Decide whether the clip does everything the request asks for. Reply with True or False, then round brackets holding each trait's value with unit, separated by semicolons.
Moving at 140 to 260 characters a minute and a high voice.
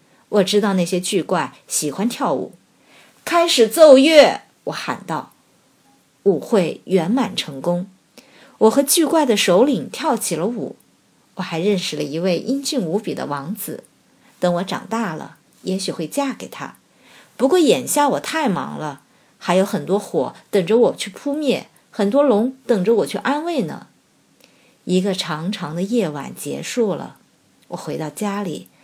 True (215 characters per minute; 205 Hz)